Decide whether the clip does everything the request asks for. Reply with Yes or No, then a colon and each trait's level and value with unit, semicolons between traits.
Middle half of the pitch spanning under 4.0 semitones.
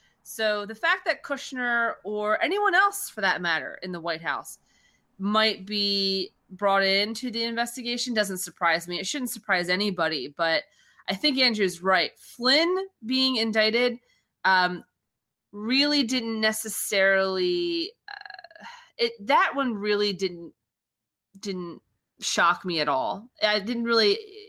No: average, 5.3 semitones